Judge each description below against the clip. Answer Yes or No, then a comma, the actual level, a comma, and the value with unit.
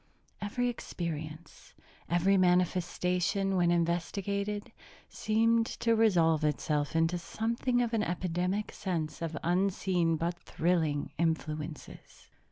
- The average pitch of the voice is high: No, medium, 175 Hz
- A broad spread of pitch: No, average, 3.4 semitones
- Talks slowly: Yes, slow, 100 wpm